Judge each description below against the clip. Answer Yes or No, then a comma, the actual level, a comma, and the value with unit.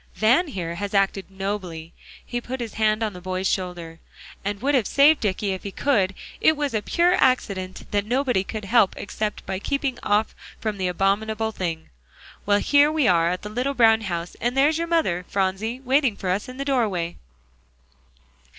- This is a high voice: Yes, high, 210 Hz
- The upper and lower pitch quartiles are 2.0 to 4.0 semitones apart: No, average, 5.2 semitones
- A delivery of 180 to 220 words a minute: Yes, average, 185 wpm